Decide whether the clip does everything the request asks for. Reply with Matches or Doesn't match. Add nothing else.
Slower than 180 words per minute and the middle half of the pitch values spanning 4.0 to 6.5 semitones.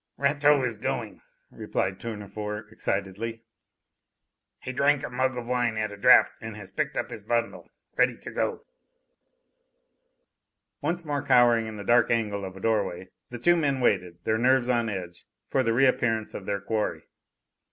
Doesn't match